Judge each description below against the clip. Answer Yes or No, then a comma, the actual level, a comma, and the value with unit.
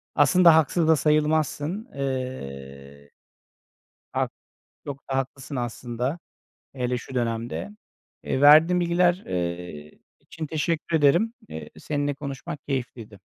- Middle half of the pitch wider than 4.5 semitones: Yes, average, 5.2 semitones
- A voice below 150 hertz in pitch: Yes, medium, 140 Hz